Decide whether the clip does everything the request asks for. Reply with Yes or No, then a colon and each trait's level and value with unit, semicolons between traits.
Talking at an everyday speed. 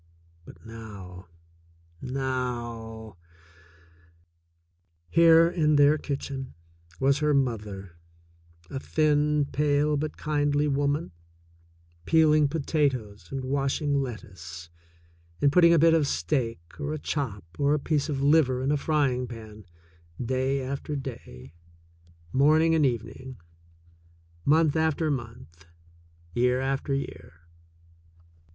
No: slow, 110 wpm